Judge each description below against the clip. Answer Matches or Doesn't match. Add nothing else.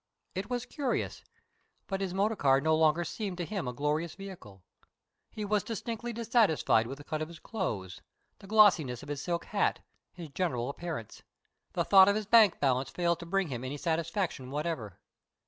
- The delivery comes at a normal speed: Matches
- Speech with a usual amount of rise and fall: Doesn't match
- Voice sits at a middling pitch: Matches